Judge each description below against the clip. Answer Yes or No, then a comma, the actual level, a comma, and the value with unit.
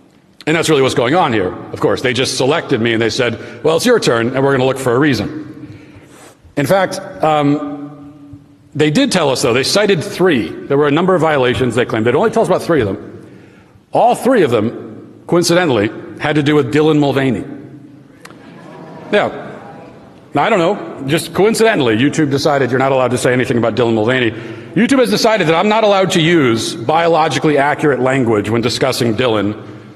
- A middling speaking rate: Yes, average, 195 wpm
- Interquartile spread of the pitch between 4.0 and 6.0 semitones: Yes, average, 4.6 semitones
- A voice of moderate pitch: Yes, medium, 145 Hz